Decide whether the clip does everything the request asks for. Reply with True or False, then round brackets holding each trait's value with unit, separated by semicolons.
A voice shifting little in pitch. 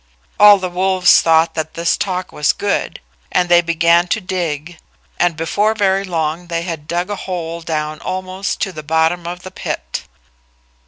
True (2.3 semitones)